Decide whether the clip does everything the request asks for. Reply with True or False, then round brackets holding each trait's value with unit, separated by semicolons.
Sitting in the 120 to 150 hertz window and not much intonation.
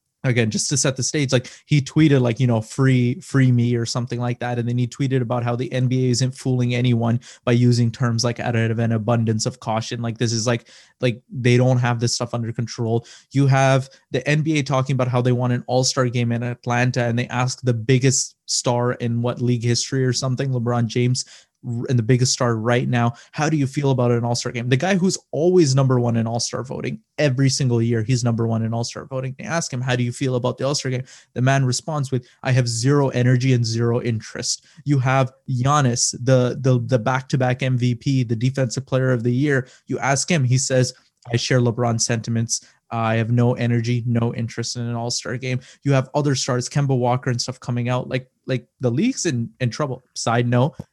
True (125 Hz; 1.7 semitones)